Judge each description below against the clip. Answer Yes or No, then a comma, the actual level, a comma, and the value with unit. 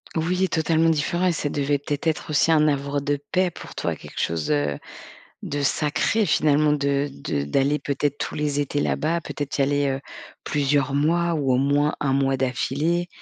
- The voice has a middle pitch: Yes, medium, 145 Hz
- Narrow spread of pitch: Yes, narrow, 2.1 semitones